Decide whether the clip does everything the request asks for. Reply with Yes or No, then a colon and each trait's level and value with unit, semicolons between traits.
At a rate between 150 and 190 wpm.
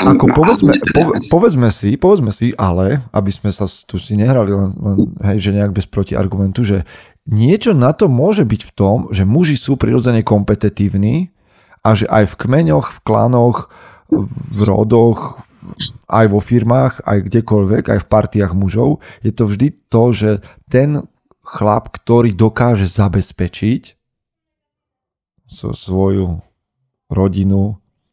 No: average, 135 wpm